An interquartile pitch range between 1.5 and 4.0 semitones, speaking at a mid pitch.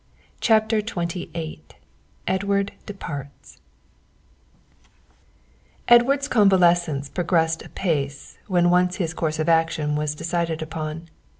Yes: average, 3.6 semitones; medium, 170 Hz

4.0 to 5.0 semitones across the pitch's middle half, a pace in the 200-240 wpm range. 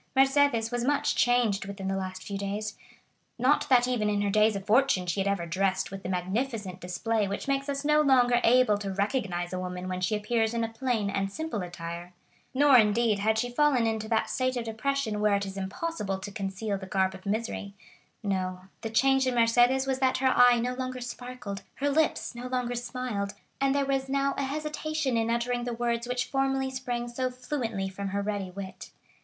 Yes: average, 4.5 semitones; fast, 205 wpm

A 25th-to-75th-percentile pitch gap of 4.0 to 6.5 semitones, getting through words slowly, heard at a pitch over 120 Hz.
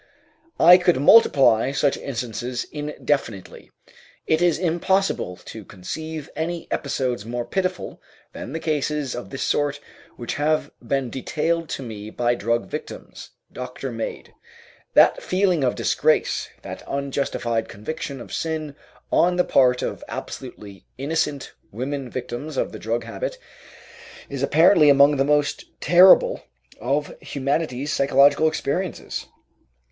Yes: average, 4.4 semitones; slow, 125 wpm; medium, 140 Hz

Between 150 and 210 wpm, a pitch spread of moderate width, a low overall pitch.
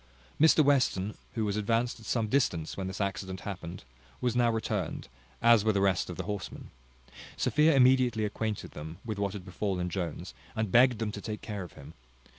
Yes: average, 190 wpm; average, 3.7 semitones; low, 105 Hz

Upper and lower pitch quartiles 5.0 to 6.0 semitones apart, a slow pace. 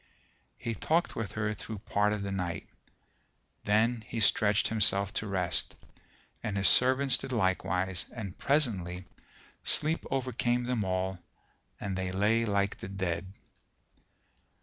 No: average, 3.7 semitones; slow, 130 wpm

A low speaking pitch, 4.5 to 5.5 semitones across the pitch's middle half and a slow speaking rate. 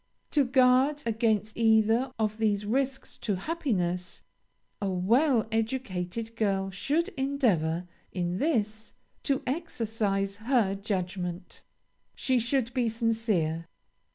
No: high, 220 Hz; average, 4.8 semitones; slow, 105 wpm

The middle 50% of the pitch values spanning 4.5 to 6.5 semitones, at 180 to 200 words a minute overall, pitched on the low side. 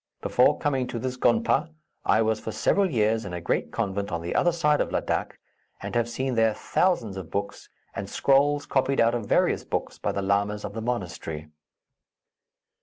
Yes: average, 5.1 semitones; average, 185 wpm; low, 115 Hz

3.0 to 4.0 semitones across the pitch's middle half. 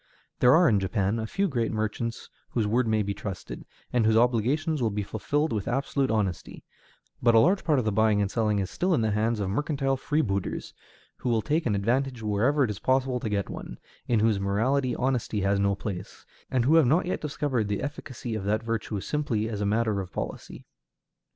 No: average, 4.4 semitones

